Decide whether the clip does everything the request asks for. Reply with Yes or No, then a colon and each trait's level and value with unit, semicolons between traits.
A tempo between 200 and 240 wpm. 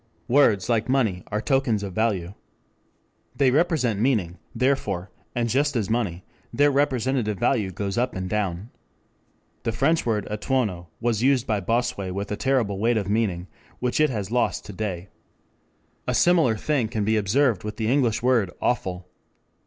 No: average, 160 wpm